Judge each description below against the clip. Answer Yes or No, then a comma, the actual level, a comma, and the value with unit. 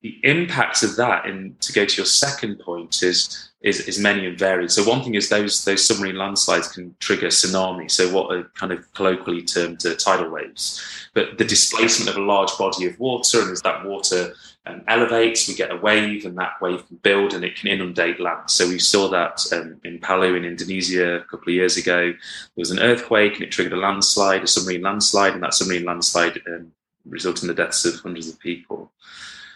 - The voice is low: Yes, very low, 95 Hz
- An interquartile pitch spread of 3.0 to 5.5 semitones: No, narrow, 2.6 semitones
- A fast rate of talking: Yes, fast, 215 wpm